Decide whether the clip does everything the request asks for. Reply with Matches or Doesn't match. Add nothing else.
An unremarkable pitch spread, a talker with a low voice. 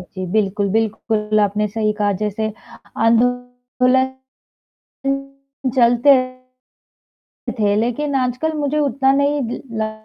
Doesn't match